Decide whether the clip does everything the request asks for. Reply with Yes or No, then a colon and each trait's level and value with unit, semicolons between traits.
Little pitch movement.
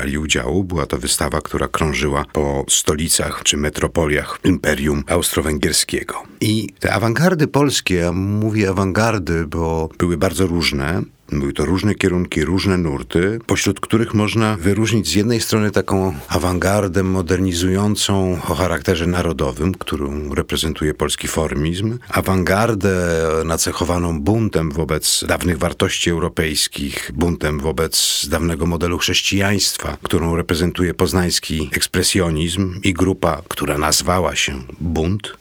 No: average, 3.2 semitones